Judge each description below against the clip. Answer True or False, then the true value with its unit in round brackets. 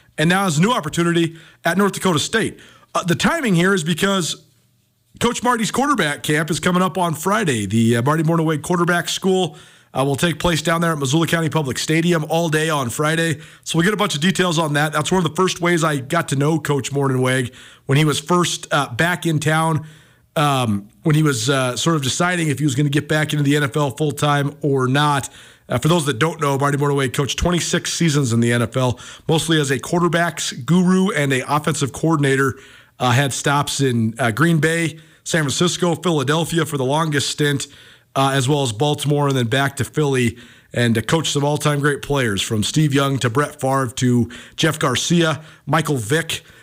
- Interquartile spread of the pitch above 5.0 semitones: False (3.5 semitones)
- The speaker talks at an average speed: False (210 wpm)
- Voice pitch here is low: False (150 Hz)